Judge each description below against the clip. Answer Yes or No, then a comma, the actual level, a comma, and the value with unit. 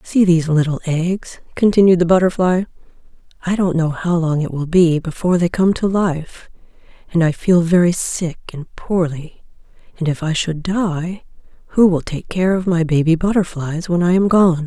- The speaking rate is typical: Yes, average, 180 wpm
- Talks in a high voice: No, medium, 170 Hz